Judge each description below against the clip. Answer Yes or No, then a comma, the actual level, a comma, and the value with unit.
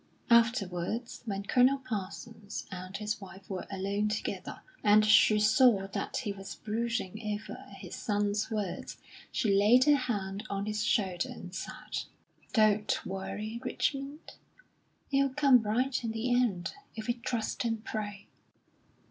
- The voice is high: Yes, high, 215 Hz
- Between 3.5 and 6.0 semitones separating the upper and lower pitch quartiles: No, average, 3.0 semitones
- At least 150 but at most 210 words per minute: No, average, 140 wpm